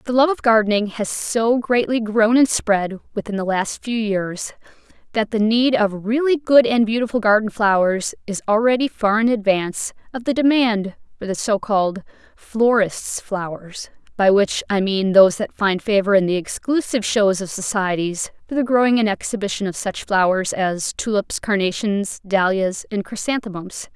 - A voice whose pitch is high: Yes, high, 215 Hz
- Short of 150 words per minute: No, average, 165 wpm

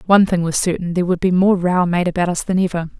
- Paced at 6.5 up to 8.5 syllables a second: Yes, 6.9 syllables/s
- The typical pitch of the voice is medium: Yes, medium, 180 Hz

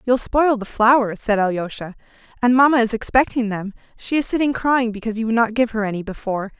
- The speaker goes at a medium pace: No, fast, 210 wpm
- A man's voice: No, female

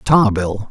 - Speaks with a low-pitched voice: Yes, low, 110 Hz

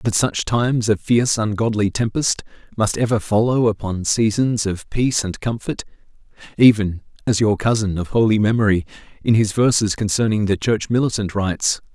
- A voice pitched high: No, low, 110 Hz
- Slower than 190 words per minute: Yes, average, 150 wpm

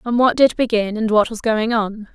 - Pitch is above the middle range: Yes, high, 225 Hz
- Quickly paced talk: Yes, fast, 250 wpm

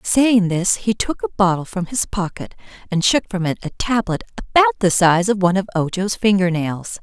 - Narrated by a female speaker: Yes, female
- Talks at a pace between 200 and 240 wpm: Yes, fast, 205 wpm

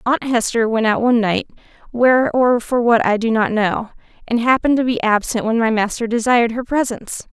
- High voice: Yes, high, 235 Hz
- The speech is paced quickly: No, average, 185 wpm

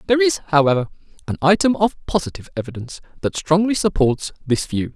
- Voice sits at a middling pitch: Yes, medium, 170 Hz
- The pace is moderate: Yes, average, 160 wpm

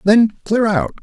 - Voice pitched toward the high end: Yes, high, 205 Hz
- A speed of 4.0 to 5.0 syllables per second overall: Yes, 4.1 syllables/s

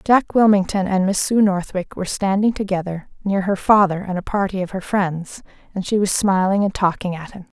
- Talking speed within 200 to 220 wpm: Yes, fast, 205 wpm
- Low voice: No, high, 190 Hz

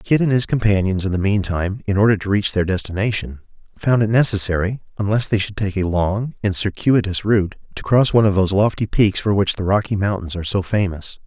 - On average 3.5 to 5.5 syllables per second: No, 5.9 syllables/s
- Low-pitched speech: Yes, low, 100 Hz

